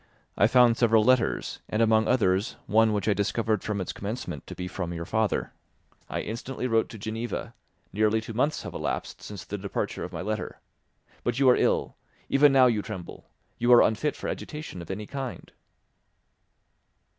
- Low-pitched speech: Yes, low, 110 Hz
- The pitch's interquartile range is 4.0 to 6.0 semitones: No, average, 2.9 semitones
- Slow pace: No, average, 180 wpm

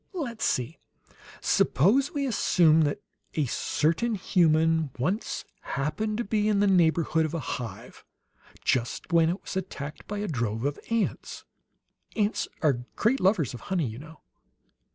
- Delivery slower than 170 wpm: Yes, average, 150 wpm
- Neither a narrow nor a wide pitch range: No, wide, 6.2 semitones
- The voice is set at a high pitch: No, medium, 165 Hz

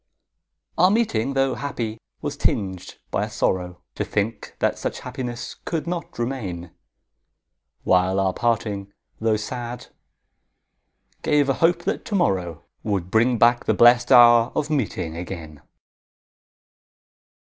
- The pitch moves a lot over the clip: Yes, wide, 5.9 semitones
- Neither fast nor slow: No, slow, 125 wpm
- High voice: No, low, 115 Hz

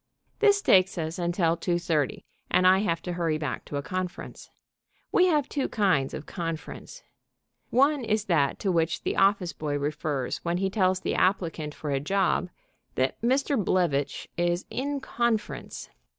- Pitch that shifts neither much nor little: Yes, average, 4.7 semitones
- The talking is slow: No, average, 165 wpm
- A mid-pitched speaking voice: Yes, medium, 180 Hz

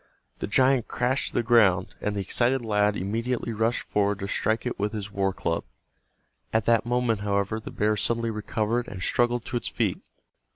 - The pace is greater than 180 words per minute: Yes, average, 190 wpm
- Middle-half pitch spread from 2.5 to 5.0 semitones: Yes, average, 2.8 semitones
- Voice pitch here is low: Yes, low, 110 Hz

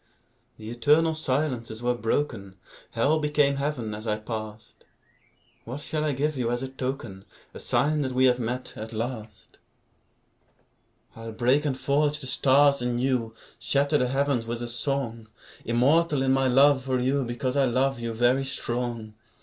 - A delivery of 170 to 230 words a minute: No, average, 160 wpm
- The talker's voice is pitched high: No, low, 130 Hz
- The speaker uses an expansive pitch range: No, average, 3.2 semitones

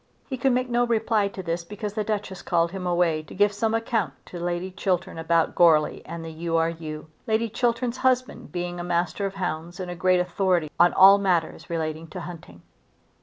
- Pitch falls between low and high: Yes, medium, 180 Hz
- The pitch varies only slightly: No, average, 3.8 semitones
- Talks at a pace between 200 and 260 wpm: Yes, fast, 205 wpm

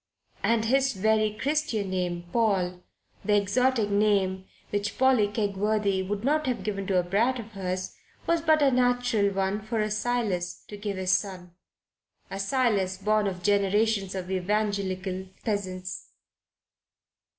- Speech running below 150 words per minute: Yes, average, 140 wpm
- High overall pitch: Yes, high, 205 Hz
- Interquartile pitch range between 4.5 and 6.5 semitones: No, average, 3.0 semitones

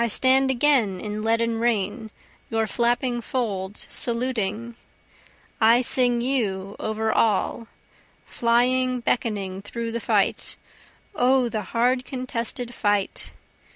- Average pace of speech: No, slow, 110 wpm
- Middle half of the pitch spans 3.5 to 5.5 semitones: No, narrow, 2.6 semitones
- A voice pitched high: Yes, high, 235 Hz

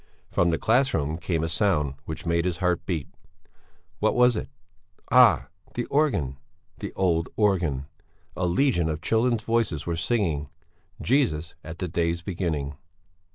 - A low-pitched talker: Yes, very low, 85 Hz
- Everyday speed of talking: Yes, average, 150 wpm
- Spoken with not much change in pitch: No, average, 5.2 semitones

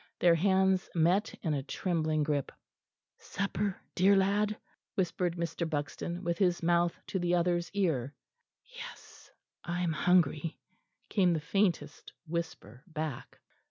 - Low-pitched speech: No, medium, 175 Hz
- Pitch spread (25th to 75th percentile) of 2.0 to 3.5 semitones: Yes, average, 3.2 semitones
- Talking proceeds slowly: Yes, slow, 125 wpm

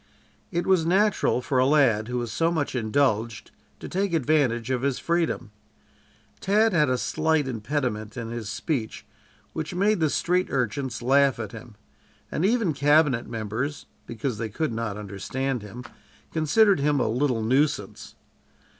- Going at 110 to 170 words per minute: Yes, average, 155 wpm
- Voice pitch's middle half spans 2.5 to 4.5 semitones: No, wide, 5.5 semitones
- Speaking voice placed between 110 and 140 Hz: Yes, low, 135 Hz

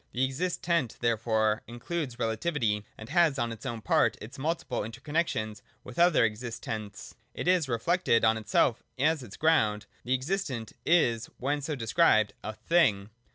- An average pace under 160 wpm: Yes, average, 150 wpm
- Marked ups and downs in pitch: Yes, wide, 6.2 semitones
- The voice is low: Yes, low, 120 Hz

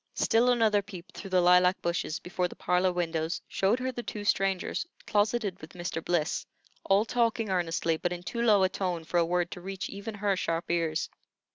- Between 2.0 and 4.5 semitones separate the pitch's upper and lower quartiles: Yes, average, 3.0 semitones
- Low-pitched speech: No, medium, 185 Hz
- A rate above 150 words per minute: Yes, average, 200 wpm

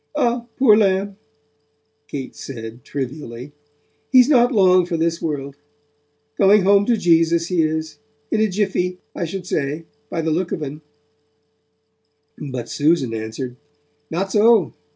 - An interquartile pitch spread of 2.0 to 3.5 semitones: No, wide, 5.4 semitones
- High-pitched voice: No, medium, 170 Hz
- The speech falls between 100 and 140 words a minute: Yes, slow, 135 wpm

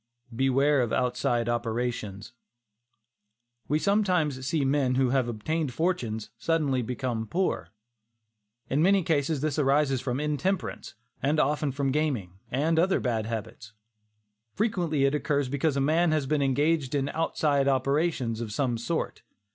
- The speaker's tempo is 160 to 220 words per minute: No, average, 140 wpm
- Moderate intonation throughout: Yes, average, 3.9 semitones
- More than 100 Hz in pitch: Yes, medium, 140 Hz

